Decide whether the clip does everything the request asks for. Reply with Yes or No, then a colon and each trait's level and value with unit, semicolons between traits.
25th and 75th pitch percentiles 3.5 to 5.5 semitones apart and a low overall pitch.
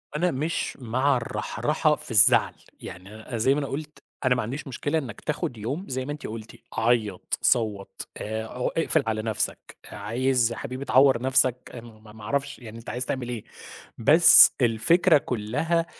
Yes: average, 4.1 semitones; low, 125 Hz